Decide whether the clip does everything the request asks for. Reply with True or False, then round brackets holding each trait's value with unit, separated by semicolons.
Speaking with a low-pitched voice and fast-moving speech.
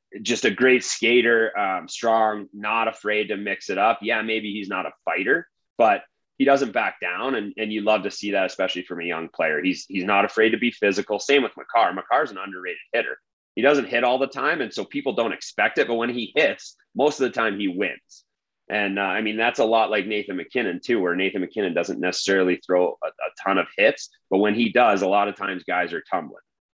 True (110 Hz; 235 wpm)